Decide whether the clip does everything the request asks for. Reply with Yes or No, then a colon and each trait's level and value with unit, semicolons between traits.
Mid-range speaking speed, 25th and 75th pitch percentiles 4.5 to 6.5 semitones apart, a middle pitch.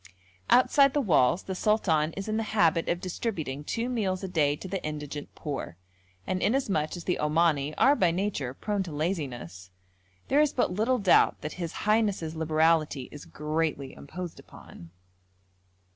Yes: average, 160 wpm; average, 5.3 semitones; medium, 170 Hz